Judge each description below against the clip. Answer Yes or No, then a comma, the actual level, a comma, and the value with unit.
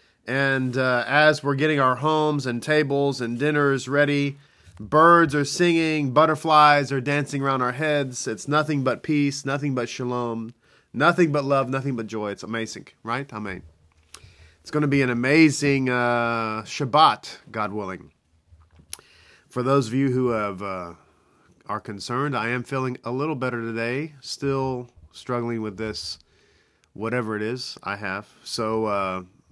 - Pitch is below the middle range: Yes, low, 130 Hz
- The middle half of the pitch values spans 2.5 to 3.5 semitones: No, average, 4.5 semitones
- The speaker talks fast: No, average, 155 wpm